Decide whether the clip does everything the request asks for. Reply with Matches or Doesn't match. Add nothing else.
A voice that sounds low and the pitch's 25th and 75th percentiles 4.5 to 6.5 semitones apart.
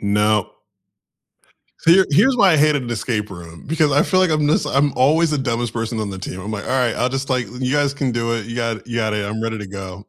Matches